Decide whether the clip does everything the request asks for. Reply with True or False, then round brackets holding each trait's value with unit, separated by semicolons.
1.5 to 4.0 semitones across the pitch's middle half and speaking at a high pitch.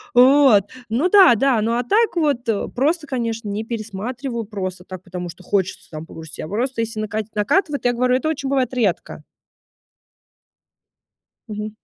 False (4.5 semitones; 230 Hz)